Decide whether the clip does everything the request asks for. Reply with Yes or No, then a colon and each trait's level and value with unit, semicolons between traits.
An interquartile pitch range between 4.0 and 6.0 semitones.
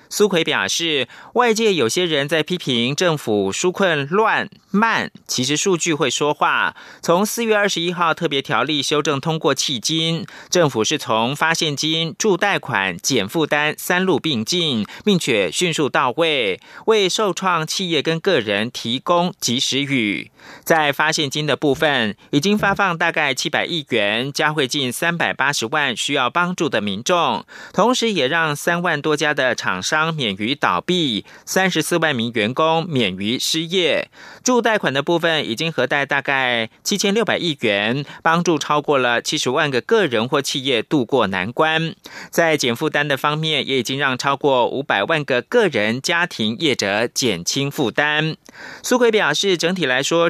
Yes: average, 4.4 semitones